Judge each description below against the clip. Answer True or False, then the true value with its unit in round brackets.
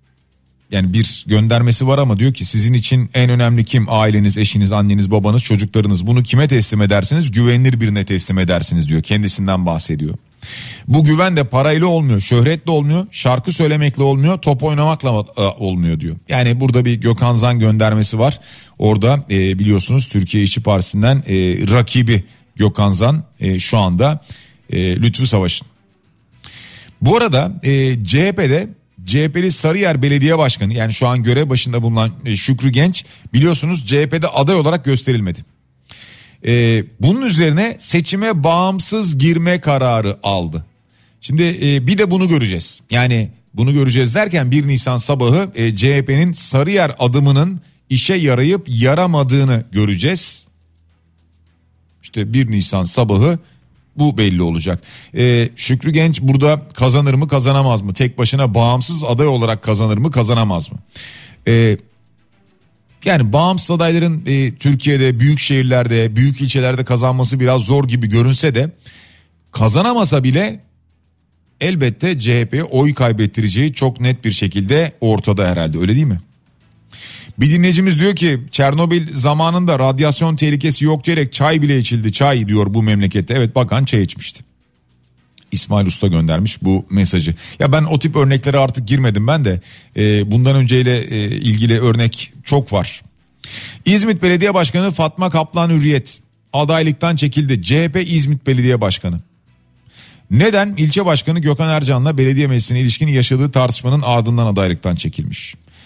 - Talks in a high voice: False (125 Hz)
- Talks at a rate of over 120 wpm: True (130 wpm)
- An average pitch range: False (5.7 semitones)